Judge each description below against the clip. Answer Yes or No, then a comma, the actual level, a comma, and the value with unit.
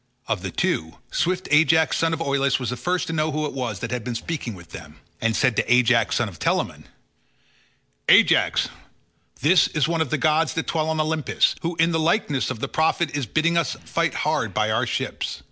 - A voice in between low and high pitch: Yes, medium, 155 Hz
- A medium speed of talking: No, fast, 215 wpm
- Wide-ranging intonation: No, average, 4.6 semitones